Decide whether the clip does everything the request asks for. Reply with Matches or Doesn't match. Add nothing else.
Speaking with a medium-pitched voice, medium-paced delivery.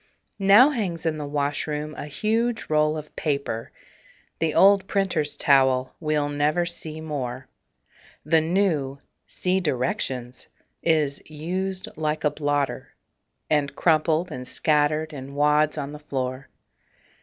Doesn't match